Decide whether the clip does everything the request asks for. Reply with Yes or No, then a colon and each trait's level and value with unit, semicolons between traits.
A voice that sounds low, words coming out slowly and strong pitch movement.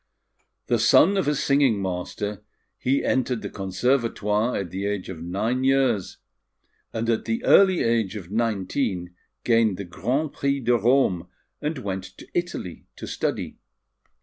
No: low, 115 Hz; average, 150 wpm; wide, 5.7 semitones